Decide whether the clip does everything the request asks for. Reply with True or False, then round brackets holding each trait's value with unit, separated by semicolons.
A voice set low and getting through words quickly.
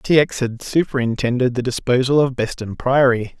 False (125 Hz; 160 wpm)